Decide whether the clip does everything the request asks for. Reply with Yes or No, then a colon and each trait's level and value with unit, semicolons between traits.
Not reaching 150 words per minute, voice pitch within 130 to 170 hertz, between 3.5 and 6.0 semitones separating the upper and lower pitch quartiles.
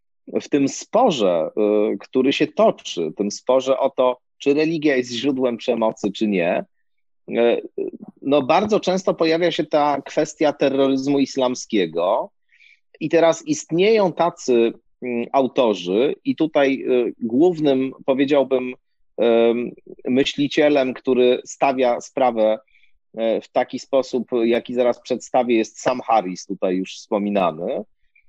Yes: slow, 110 wpm; low, 135 Hz; average, 4.4 semitones